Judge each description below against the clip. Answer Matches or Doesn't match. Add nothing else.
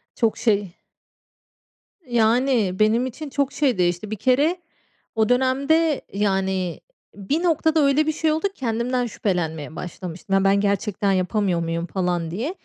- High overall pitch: Matches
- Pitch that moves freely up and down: Matches